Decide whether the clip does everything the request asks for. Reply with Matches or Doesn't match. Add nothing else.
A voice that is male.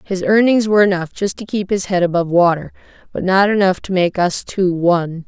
Doesn't match